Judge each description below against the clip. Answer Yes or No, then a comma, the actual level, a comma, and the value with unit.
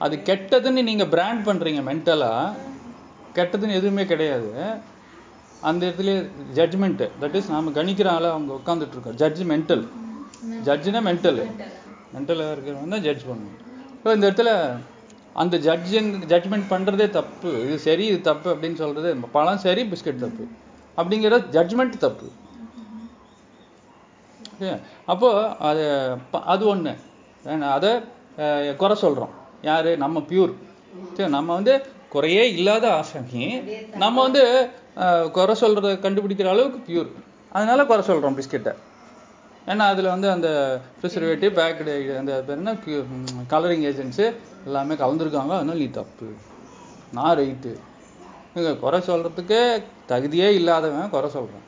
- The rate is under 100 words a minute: No, average, 110 wpm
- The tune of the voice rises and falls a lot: Yes, wide, 5.8 semitones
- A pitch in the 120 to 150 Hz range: No, medium, 175 Hz